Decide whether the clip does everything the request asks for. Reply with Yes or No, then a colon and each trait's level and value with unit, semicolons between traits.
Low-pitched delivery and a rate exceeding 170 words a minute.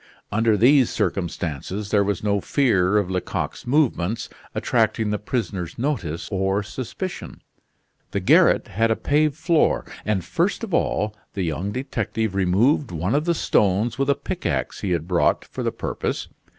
No: low, 105 Hz; average, 155 wpm